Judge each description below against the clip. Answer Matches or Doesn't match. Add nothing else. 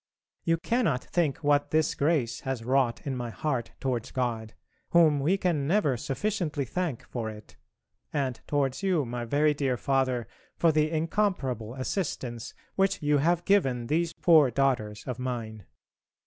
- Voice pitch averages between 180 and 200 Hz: Doesn't match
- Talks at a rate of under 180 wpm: Matches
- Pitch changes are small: Doesn't match